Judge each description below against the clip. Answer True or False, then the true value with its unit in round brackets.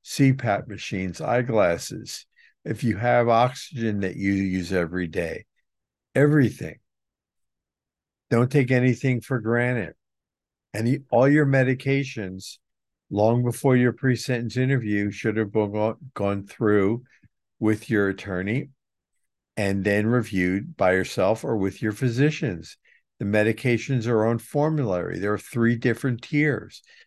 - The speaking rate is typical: False (120 wpm)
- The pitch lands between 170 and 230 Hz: False (115 Hz)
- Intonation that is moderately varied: True (4.1 semitones)